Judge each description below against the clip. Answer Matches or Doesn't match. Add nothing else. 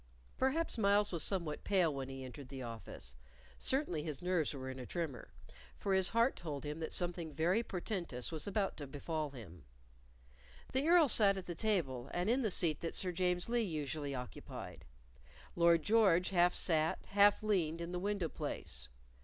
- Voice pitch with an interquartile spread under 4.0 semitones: Doesn't match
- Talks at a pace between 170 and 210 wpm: Matches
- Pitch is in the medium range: Matches